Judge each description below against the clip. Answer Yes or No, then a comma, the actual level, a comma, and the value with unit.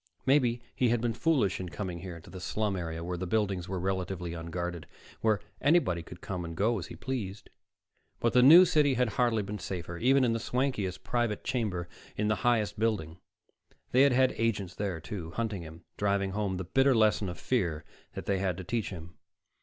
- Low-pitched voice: Yes, low, 100 Hz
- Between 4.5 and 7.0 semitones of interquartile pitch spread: Yes, average, 5.0 semitones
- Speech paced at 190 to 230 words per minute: Yes, average, 200 wpm